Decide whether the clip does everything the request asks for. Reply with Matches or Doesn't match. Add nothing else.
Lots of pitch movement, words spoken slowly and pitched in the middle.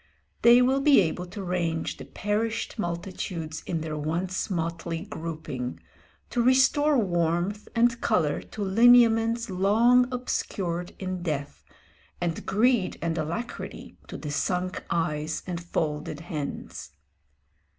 Matches